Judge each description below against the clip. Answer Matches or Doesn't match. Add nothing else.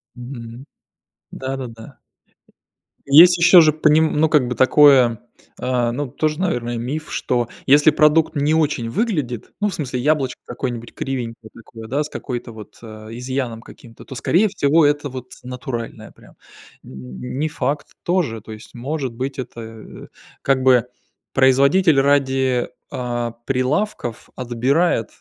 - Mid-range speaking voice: Doesn't match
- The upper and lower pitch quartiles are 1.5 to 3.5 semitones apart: Doesn't match